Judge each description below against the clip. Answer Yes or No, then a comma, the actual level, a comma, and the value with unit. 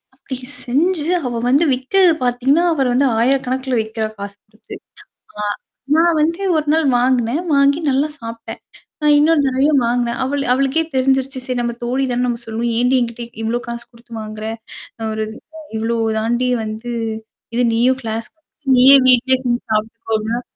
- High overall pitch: Yes, very high, 250 Hz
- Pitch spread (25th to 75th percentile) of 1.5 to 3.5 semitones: Yes, average, 2.9 semitones